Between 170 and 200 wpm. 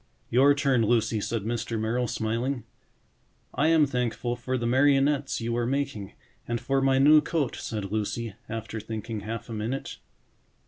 No: average, 155 wpm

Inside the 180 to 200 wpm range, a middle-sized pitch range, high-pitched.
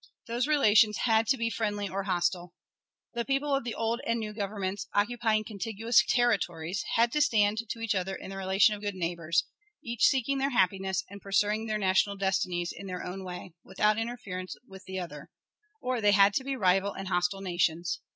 Yes: average, 190 wpm; average, 3.4 semitones; high, 205 Hz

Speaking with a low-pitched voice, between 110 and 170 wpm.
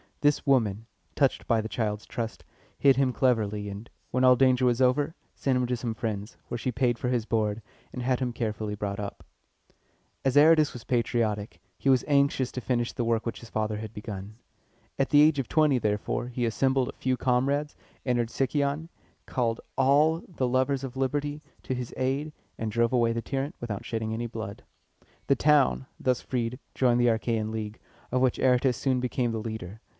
No: low, 125 Hz; average, 190 wpm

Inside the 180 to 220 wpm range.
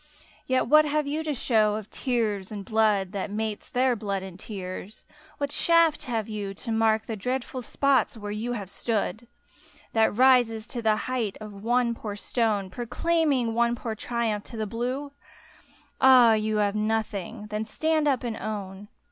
No: average, 170 wpm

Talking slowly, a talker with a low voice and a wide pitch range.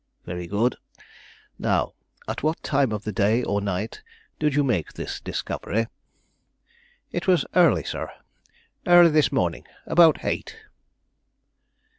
Yes: slow, 125 wpm; low, 125 Hz; wide, 7.4 semitones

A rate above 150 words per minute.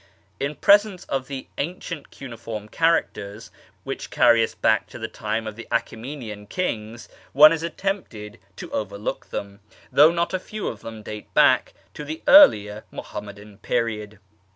Yes: average, 160 wpm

